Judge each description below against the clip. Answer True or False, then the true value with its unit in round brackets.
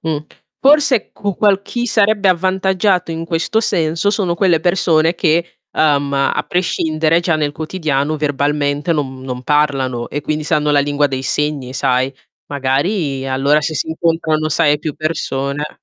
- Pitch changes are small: False (3.3 semitones)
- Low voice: False (155 Hz)